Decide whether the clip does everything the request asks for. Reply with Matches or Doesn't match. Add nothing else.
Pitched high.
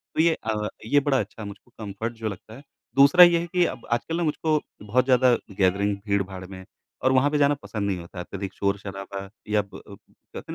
Doesn't match